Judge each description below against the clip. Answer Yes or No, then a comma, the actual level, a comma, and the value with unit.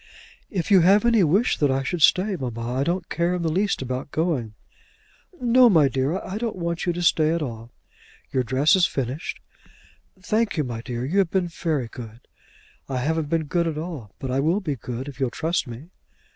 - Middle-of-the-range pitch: Yes, medium, 160 Hz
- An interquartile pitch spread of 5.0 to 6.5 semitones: Yes, wide, 5.6 semitones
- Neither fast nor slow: No, fast, 210 wpm